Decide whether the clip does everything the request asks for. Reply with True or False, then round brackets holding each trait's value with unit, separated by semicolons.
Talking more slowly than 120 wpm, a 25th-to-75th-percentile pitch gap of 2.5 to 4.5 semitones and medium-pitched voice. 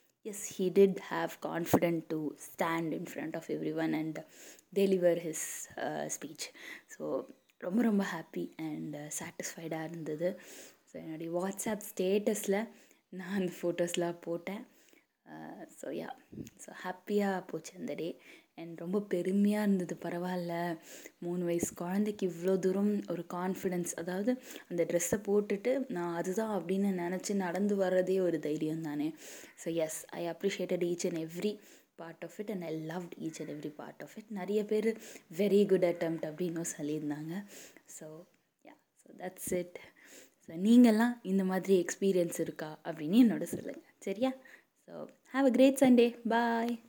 False (130 wpm; 3.5 semitones; 180 Hz)